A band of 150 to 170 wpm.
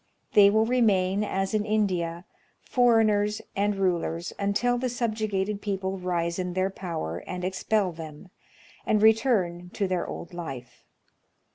No: slow, 135 wpm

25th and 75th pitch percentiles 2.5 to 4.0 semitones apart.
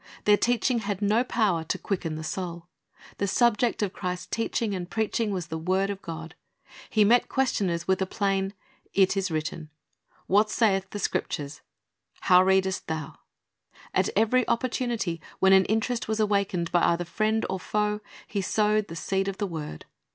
Yes: average, 3.3 semitones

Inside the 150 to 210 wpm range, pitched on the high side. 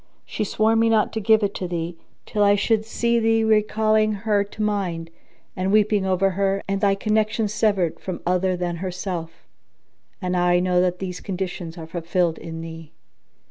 Yes: average, 180 wpm; high, 195 Hz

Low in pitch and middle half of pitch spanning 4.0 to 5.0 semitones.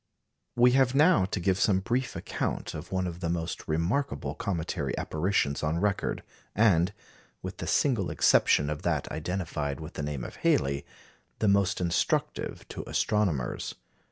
Yes: very low, 90 Hz; average, 4.7 semitones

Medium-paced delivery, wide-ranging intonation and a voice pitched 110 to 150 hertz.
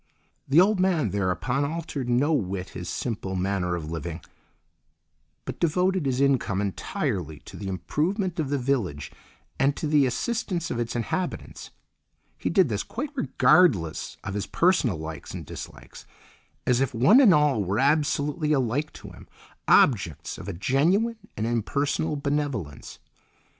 Yes: average, 150 wpm; wide, 8.2 semitones; low, 135 Hz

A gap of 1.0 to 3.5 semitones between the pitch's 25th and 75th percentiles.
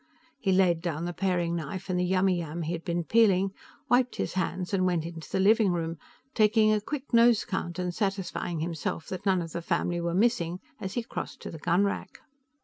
Yes: average, 2.8 semitones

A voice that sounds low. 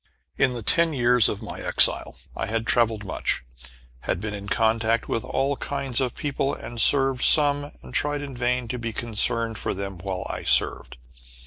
Yes: low, 120 Hz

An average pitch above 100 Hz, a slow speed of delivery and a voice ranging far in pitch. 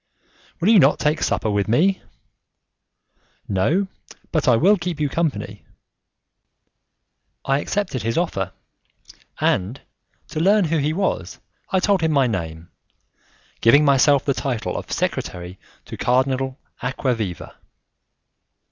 Yes: medium, 140 Hz; slow, 120 wpm; wide, 6.5 semitones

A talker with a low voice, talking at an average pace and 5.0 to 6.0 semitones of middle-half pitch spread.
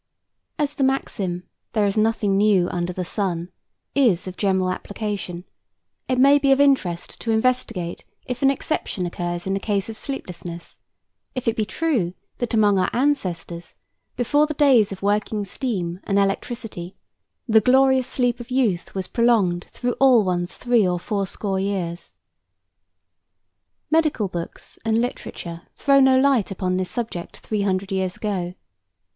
No: high, 205 Hz; average, 155 wpm; wide, 5.4 semitones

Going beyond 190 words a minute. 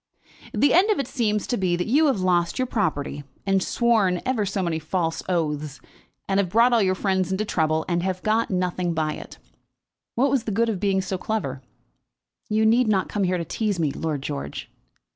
Yes: fast, 205 wpm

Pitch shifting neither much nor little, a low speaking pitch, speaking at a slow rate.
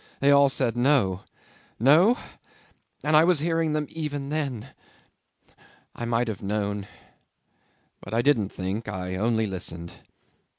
No: wide, 6.4 semitones; low, 120 Hz; slow, 130 wpm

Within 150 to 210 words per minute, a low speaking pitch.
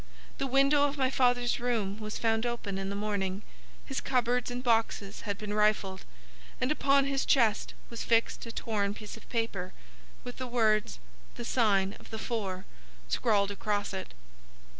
No: average, 165 wpm; high, 225 Hz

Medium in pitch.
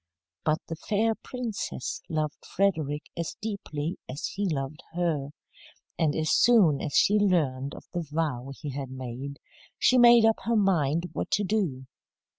Yes: medium, 160 Hz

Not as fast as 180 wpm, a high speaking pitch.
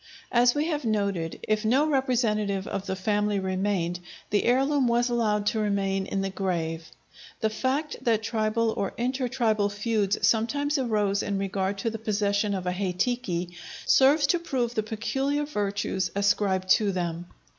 Yes: average, 160 wpm; high, 210 Hz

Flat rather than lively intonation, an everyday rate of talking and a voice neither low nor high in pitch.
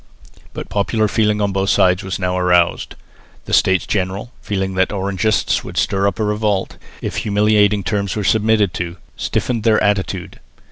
No: narrow, 2.0 semitones; average, 170 wpm; low, 100 Hz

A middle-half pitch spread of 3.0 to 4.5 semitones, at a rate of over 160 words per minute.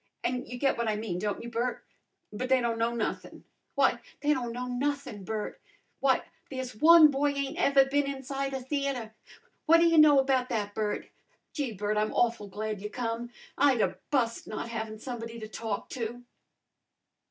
Yes: average, 3.7 semitones; average, 185 wpm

